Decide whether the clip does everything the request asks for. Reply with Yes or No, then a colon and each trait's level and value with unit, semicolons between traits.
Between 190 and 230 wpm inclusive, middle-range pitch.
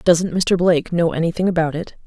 Yes: fast, 205 wpm; medium, 170 Hz